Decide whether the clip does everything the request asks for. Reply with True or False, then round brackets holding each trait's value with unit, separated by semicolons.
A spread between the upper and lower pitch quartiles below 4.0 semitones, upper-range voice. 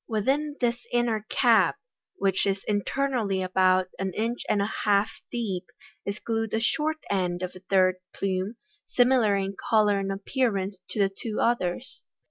True (3.6 semitones; 205 Hz)